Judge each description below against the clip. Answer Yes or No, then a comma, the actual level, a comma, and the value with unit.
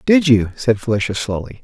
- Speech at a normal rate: Yes, average, 185 wpm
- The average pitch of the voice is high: No, low, 120 Hz